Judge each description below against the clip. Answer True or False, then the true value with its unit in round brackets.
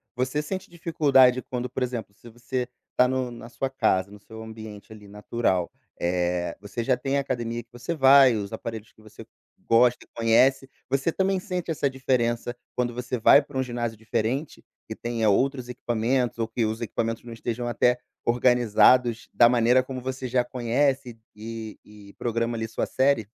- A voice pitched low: True (120 Hz)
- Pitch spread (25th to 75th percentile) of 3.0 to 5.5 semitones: False (2.6 semitones)